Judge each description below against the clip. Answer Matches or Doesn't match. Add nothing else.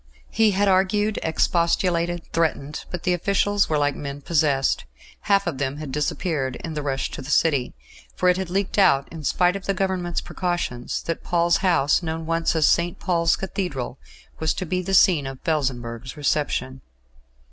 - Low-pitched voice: Doesn't match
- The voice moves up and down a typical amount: Matches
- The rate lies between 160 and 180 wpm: Matches